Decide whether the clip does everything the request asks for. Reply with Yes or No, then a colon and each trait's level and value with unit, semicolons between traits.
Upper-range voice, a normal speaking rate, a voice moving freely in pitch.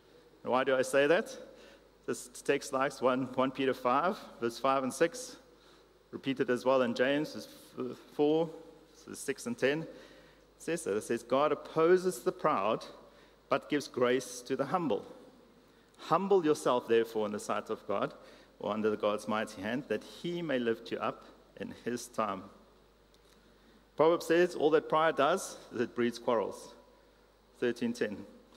No: medium, 145 Hz; average, 155 wpm; wide, 6.9 semitones